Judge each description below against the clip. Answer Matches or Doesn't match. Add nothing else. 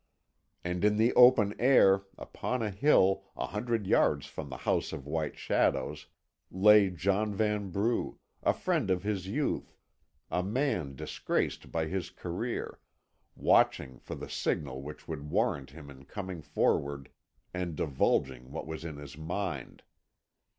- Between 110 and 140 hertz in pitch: Doesn't match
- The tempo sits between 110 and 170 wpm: Matches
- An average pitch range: Doesn't match